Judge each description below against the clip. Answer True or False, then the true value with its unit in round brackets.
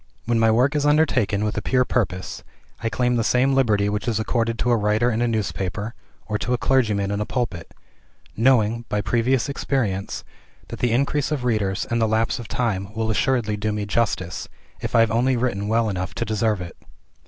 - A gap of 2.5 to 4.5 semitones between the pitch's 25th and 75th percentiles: True (2.8 semitones)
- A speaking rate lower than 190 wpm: False (205 wpm)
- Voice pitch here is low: True (115 Hz)